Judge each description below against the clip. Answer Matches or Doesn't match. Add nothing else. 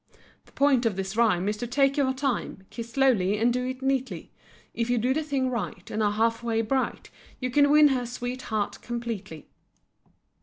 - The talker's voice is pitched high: Matches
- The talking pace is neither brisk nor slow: Matches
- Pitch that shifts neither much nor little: Matches